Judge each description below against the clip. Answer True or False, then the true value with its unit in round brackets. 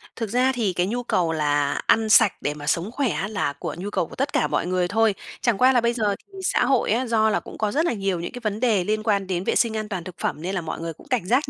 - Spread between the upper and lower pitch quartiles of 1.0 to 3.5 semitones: False (4.7 semitones)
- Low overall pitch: False (210 Hz)